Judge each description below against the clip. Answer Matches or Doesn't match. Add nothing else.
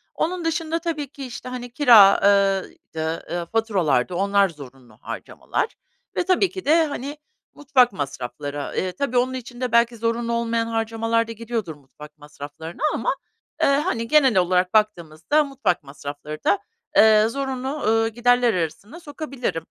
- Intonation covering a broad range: Matches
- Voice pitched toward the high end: Matches